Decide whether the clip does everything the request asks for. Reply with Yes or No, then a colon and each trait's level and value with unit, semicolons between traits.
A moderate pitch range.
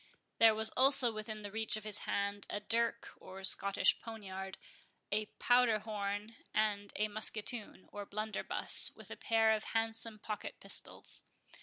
No: narrow, 1.6 semitones